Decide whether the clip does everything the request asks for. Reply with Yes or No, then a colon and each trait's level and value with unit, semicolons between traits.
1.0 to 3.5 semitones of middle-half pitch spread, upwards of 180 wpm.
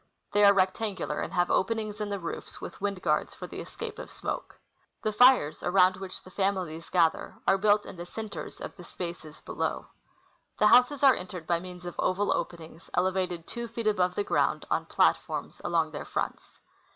Yes: average, 3.1 semitones; average, 190 wpm